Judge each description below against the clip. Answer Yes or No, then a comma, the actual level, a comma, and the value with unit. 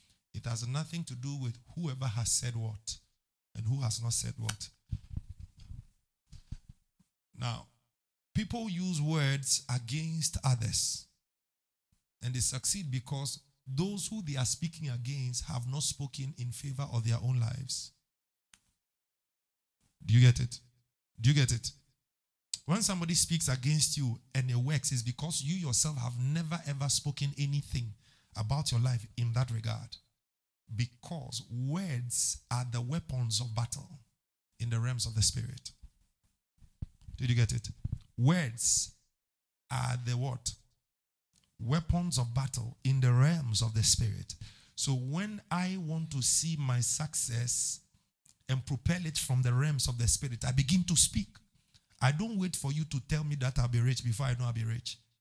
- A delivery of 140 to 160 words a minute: Yes, average, 155 wpm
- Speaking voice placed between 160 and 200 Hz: No, low, 125 Hz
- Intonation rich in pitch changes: No, average, 3.5 semitones